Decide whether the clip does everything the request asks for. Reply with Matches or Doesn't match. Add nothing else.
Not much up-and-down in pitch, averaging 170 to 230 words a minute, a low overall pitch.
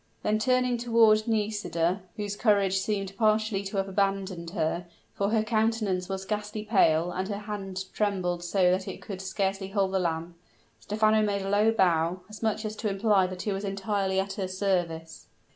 Doesn't match